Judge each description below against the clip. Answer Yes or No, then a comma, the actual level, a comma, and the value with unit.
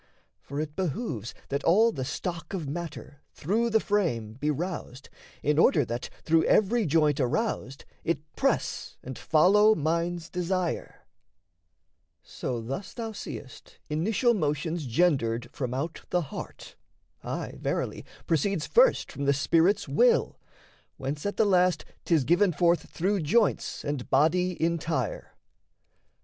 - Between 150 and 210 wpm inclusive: No, slow, 135 wpm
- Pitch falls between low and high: Yes, medium, 165 Hz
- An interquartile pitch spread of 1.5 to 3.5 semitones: No, average, 4.9 semitones